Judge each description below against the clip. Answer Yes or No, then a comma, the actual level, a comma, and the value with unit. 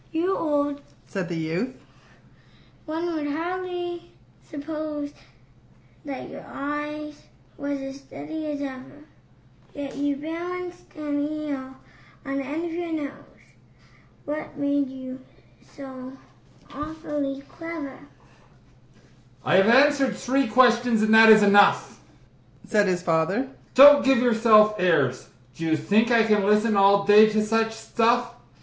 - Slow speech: Yes, slow, 130 wpm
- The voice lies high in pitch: Yes, very high, 270 Hz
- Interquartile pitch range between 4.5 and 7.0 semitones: Yes, average, 5.1 semitones